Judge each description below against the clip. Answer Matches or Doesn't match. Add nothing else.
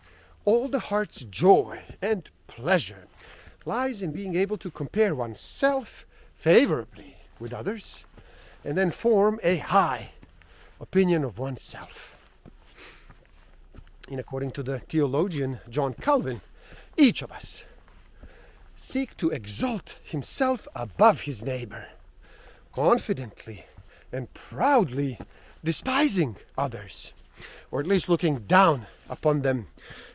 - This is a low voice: Doesn't match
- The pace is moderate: Doesn't match